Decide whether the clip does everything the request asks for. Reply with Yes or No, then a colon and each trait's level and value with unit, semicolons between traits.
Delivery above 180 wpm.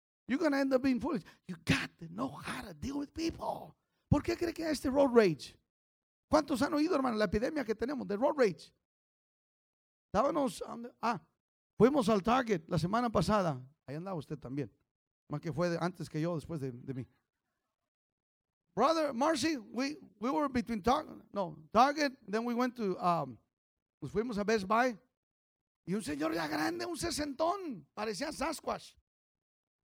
No: average, 175 wpm